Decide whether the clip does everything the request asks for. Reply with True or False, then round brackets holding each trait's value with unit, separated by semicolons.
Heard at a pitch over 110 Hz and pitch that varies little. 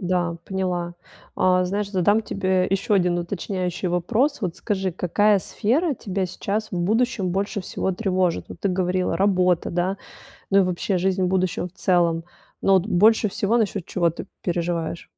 True (185 Hz; 2.1 semitones)